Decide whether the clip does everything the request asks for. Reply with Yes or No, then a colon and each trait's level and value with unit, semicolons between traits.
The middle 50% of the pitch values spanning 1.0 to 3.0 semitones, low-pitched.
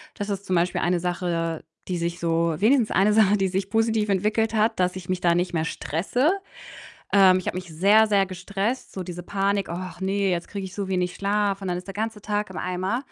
No: average, 2.7 semitones; high, 190 Hz